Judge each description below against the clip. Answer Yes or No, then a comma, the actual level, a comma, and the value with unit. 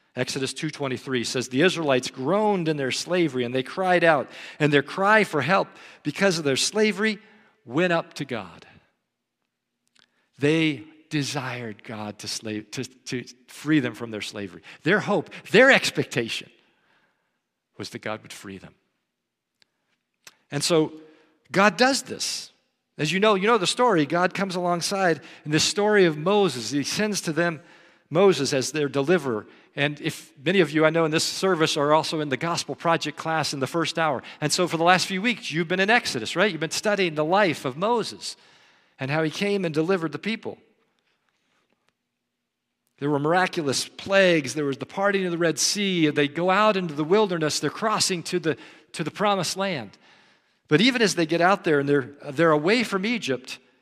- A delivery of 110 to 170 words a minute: No, average, 180 wpm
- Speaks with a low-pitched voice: No, medium, 160 Hz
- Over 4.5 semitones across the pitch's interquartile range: Yes, average, 5.2 semitones